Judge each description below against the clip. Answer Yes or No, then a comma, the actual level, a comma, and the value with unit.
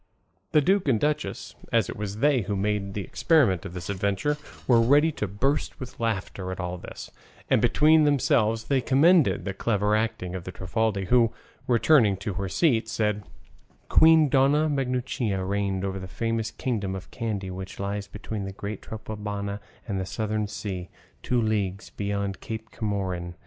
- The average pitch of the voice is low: Yes, low, 105 Hz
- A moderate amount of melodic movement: Yes, average, 4.2 semitones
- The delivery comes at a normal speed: Yes, average, 170 wpm